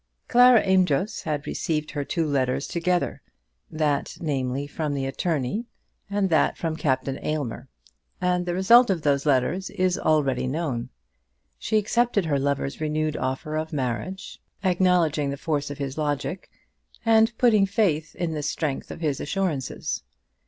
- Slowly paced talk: No, average, 145 wpm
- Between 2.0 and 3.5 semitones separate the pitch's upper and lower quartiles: No, average, 4.6 semitones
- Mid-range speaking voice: Yes, medium, 155 Hz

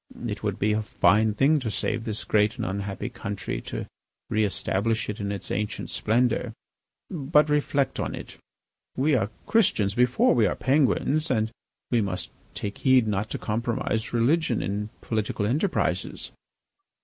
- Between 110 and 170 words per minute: Yes, average, 155 wpm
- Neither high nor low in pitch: No, low, 110 Hz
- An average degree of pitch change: Yes, average, 3.9 semitones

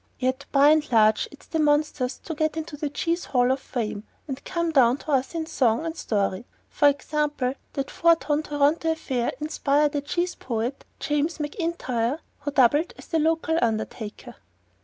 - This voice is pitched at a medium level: No, very high, 290 Hz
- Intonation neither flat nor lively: Yes, average, 3.8 semitones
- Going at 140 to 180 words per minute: Yes, average, 175 wpm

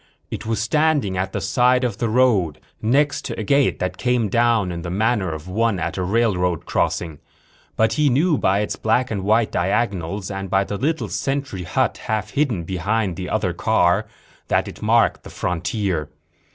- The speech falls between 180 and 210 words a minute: Yes, average, 185 wpm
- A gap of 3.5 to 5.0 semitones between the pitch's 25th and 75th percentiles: Yes, average, 4.7 semitones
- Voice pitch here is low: Yes, low, 105 Hz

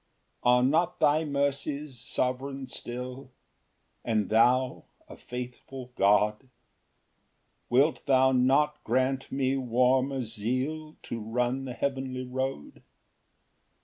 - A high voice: No, low, 130 Hz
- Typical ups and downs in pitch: No, narrow, 1.8 semitones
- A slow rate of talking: Yes, slow, 105 wpm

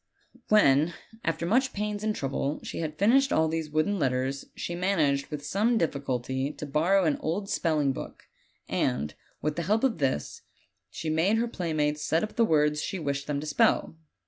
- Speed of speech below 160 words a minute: No, average, 185 wpm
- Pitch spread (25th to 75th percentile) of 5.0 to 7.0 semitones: Yes, wide, 5.5 semitones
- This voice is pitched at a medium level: Yes, medium, 155 Hz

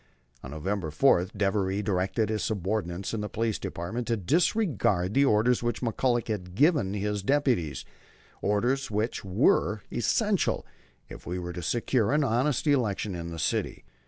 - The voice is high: No, low, 105 Hz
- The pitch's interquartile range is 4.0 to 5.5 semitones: Yes, average, 4.6 semitones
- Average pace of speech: Yes, average, 160 wpm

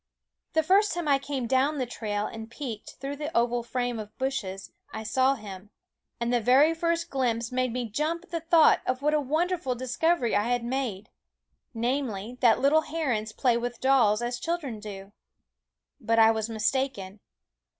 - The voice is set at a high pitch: Yes, very high, 250 Hz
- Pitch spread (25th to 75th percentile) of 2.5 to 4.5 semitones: Yes, average, 4.2 semitones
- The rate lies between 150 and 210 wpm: Yes, average, 175 wpm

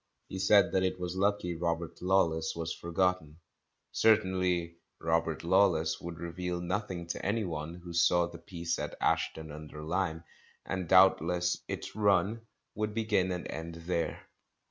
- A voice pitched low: Yes, very low, 90 Hz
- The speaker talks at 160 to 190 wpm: No, average, 145 wpm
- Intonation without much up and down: Yes, narrow, 2.1 semitones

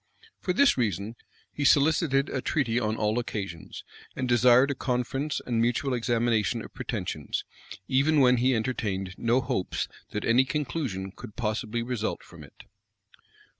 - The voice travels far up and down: No, average, 3.4 semitones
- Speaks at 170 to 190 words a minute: No, average, 145 wpm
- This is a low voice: Yes, low, 120 Hz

